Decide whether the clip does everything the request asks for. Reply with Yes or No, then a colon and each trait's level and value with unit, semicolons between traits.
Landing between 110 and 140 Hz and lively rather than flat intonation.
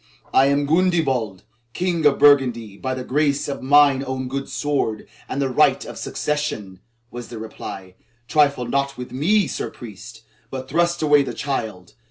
No: low, 135 Hz; average, 3.5 semitones